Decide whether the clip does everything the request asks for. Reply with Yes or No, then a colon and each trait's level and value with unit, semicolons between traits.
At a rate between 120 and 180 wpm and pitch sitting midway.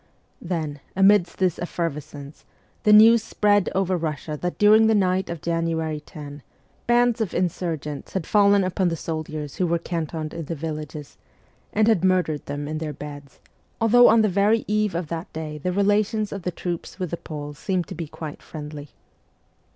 Yes: average, 175 wpm; medium, 170 Hz